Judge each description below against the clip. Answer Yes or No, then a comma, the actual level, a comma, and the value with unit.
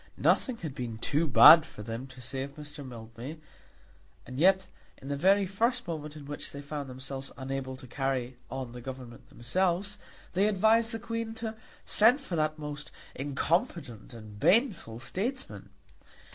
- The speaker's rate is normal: Yes, average, 160 wpm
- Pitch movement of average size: No, wide, 6.6 semitones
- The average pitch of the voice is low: No, medium, 145 Hz